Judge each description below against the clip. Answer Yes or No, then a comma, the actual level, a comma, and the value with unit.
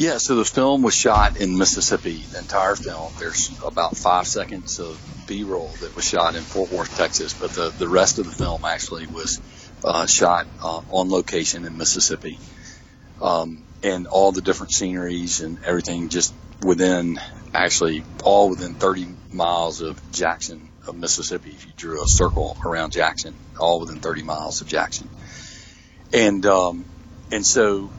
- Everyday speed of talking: Yes, average, 165 wpm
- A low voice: Yes, very low, 90 Hz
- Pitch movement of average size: No, narrow, 2.3 semitones